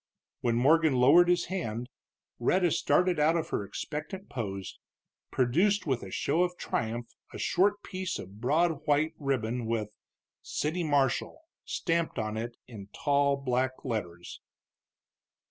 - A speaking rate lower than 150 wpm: Yes, slow, 135 wpm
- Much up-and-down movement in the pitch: Yes, wide, 6.3 semitones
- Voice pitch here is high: No, medium, 140 Hz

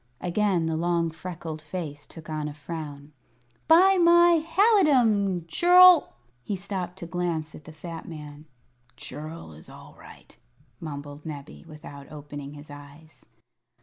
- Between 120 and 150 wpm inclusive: Yes, average, 140 wpm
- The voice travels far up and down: No, average, 4.6 semitones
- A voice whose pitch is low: No, medium, 160 Hz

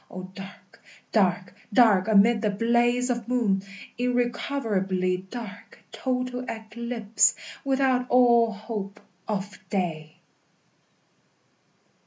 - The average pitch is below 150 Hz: No, high, 220 Hz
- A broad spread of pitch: No, average, 4.1 semitones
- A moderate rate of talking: No, slow, 90 wpm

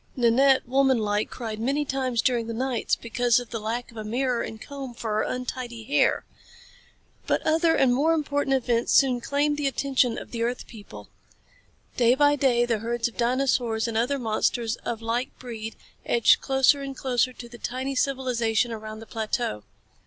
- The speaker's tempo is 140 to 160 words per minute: No, average, 180 wpm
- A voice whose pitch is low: No, high, 245 Hz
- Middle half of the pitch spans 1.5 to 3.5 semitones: Yes, average, 2.8 semitones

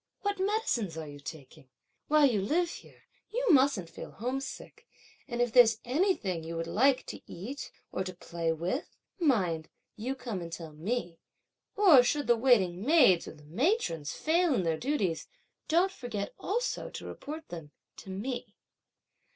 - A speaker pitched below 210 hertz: No, high, 235 Hz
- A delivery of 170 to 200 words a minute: No, average, 160 wpm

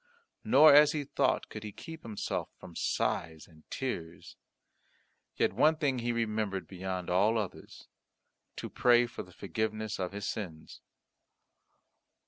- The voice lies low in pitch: Yes, low, 110 Hz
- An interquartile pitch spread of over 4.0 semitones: Yes, average, 5.1 semitones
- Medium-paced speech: No, slow, 130 wpm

